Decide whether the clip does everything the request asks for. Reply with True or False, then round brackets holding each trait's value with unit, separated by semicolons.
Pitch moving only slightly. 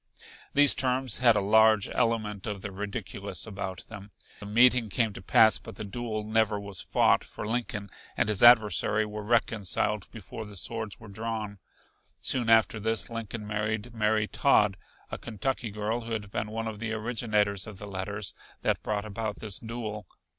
True (1.8 semitones)